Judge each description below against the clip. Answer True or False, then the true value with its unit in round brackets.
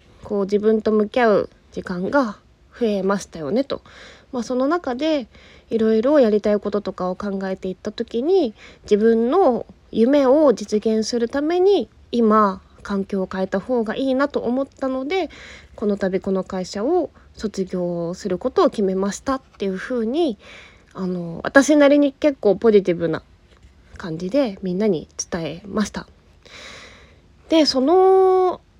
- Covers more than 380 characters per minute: False (275 characters per minute)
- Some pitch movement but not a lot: False (5.7 semitones)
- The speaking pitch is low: False (220 Hz)